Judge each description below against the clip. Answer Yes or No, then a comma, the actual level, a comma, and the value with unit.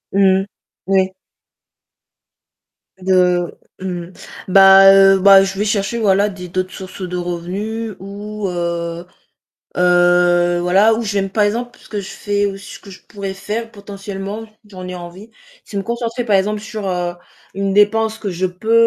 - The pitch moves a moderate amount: No, narrow, 2.3 semitones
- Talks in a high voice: Yes, high, 195 Hz